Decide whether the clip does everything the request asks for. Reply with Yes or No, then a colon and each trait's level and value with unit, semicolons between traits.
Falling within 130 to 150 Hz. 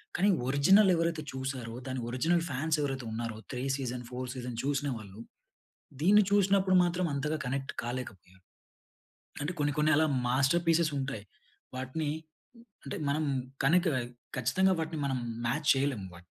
Yes: medium, 140 Hz